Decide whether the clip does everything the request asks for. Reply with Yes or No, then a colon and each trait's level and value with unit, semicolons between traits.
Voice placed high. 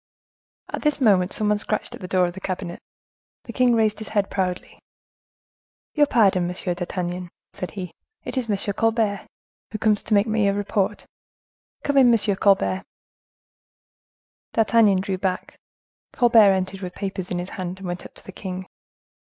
Yes: high, 195 Hz